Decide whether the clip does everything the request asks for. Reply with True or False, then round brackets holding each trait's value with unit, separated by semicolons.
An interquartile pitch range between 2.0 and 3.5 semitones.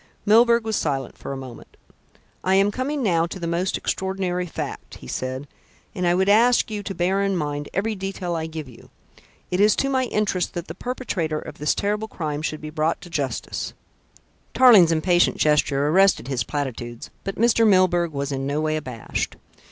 False (5.2 semitones)